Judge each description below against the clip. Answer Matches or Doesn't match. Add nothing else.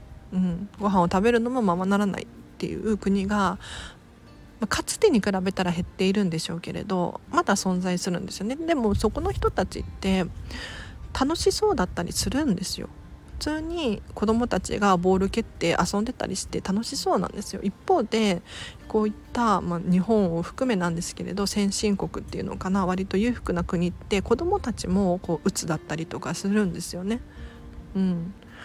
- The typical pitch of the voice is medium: Doesn't match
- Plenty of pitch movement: Doesn't match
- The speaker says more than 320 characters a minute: Matches